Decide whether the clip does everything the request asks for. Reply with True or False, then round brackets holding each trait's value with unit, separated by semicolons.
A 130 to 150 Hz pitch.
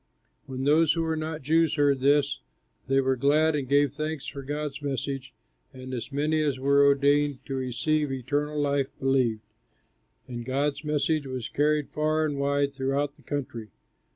True (140 Hz)